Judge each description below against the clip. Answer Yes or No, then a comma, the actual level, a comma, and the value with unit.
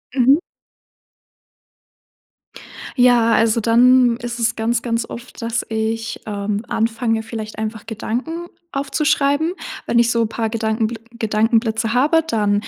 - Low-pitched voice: No, high, 230 Hz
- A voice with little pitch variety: Yes, narrow, 1.7 semitones